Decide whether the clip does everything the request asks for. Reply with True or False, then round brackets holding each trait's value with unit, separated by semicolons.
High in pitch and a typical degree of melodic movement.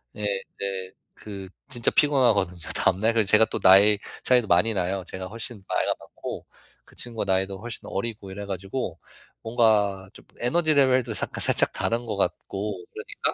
False (105 Hz; 3.5 semitones)